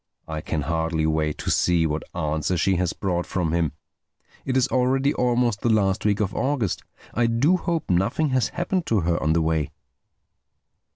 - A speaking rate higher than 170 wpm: Yes, average, 180 wpm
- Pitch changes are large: Yes, wide, 7.4 semitones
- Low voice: Yes, very low, 95 Hz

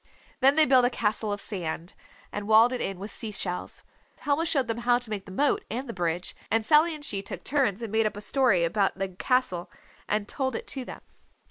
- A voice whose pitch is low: No, high, 220 Hz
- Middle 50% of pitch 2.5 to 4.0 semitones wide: No, average, 4.8 semitones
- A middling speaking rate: No, fast, 230 wpm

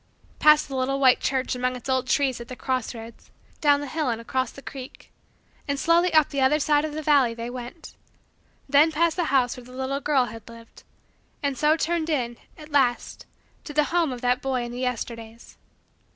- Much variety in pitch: No, average, 3.3 semitones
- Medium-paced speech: No, fast, 210 wpm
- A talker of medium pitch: No, very high, 265 Hz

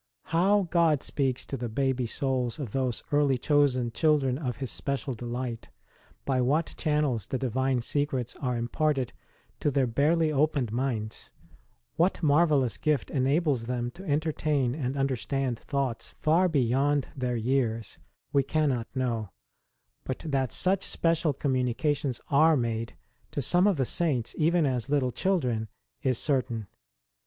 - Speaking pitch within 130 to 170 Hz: Yes, low, 135 Hz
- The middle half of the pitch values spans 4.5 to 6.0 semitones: No, average, 3.4 semitones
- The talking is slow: No, average, 145 wpm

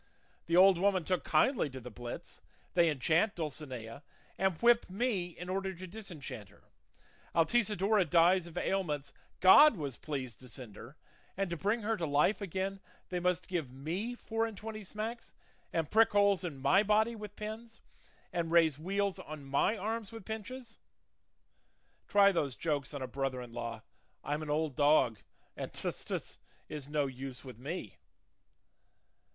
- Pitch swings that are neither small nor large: No, wide, 6.2 semitones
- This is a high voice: No, medium, 175 Hz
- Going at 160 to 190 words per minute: Yes, average, 165 wpm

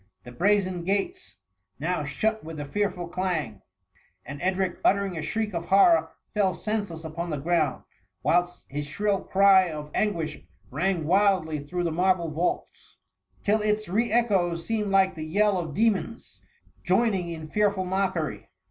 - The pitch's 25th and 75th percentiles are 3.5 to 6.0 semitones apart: Yes, average, 4.0 semitones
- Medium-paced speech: Yes, average, 165 wpm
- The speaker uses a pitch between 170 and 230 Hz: Yes, medium, 185 Hz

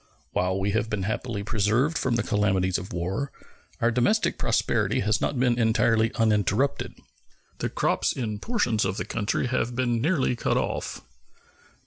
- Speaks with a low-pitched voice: Yes, low, 110 Hz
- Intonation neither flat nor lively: Yes, average, 3.4 semitones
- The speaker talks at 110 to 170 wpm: Yes, average, 155 wpm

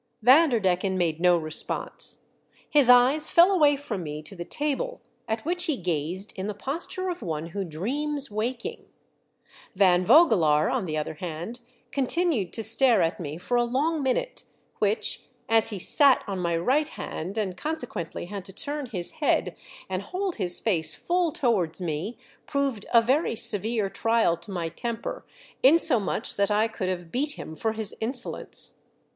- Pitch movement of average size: No, wide, 7.7 semitones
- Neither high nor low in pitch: No, high, 220 Hz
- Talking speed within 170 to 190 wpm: Yes, average, 175 wpm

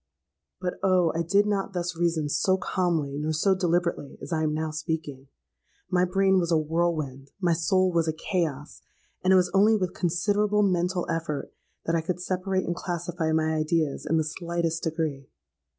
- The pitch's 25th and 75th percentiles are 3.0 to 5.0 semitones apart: No, narrow, 2.6 semitones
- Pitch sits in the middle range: Yes, medium, 170 Hz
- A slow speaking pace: No, average, 175 wpm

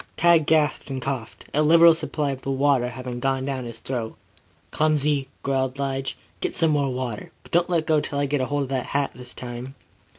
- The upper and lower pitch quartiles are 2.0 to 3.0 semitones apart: Yes, narrow, 2.6 semitones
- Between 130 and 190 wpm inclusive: No, average, 200 wpm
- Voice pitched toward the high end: No, low, 135 Hz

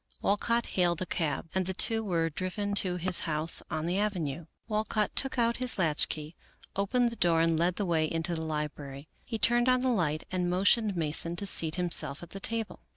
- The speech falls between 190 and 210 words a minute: Yes, fast, 205 wpm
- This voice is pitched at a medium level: Yes, medium, 180 Hz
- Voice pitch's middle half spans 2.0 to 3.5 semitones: No, average, 4.5 semitones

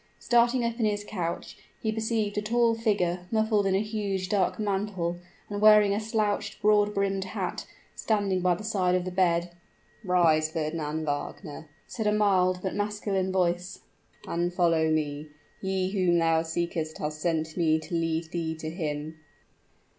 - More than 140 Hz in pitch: Yes, medium, 185 Hz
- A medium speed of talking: Yes, average, 160 wpm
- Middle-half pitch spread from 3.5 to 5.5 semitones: Yes, average, 3.9 semitones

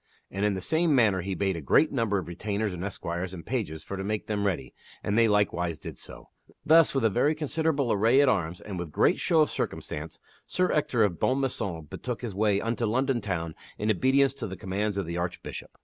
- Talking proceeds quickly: Yes, fast, 220 wpm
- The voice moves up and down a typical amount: No, wide, 5.9 semitones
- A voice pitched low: Yes, low, 105 Hz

